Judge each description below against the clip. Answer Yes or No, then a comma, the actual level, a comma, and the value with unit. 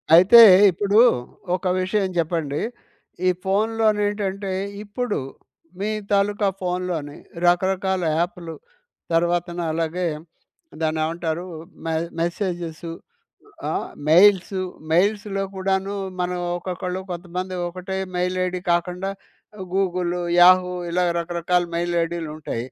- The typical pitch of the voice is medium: Yes, medium, 180 Hz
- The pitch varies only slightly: Yes, narrow, 2.1 semitones